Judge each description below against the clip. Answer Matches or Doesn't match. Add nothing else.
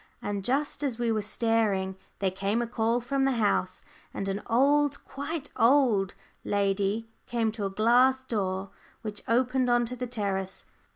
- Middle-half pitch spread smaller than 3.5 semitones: Doesn't match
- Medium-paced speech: Matches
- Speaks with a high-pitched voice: Matches